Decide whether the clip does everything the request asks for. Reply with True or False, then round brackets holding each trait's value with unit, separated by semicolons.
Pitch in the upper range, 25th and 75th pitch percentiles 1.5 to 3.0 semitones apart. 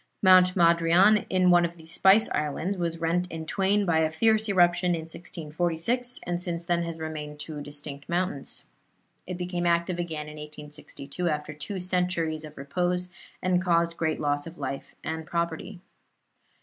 False (170 Hz; 2.4 semitones)